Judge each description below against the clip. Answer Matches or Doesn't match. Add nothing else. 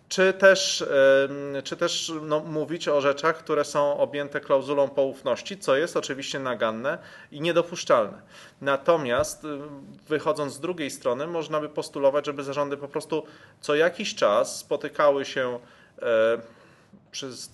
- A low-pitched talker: Doesn't match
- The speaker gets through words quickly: Doesn't match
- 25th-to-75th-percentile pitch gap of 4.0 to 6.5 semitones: Doesn't match